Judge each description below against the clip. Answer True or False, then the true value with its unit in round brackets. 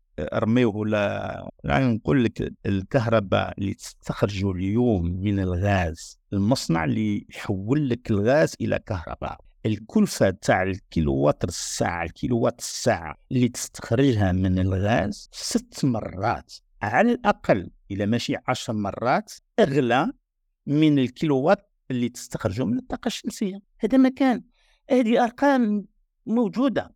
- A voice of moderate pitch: False (120 Hz)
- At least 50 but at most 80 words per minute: False (110 wpm)